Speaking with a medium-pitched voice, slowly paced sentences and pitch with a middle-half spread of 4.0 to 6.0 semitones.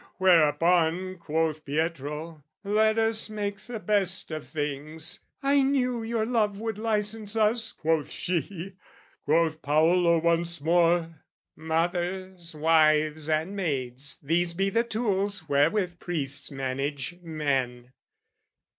Yes: medium, 170 Hz; slow, 110 wpm; average, 4.7 semitones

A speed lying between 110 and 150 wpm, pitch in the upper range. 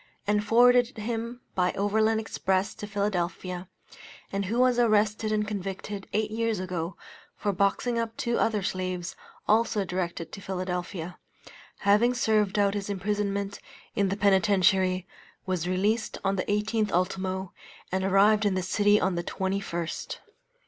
Yes: average, 140 wpm; high, 200 Hz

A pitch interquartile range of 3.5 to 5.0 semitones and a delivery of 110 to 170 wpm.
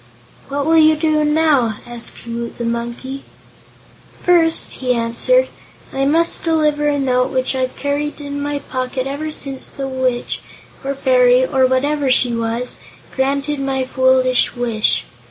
No: average, 2.8 semitones; average, 145 wpm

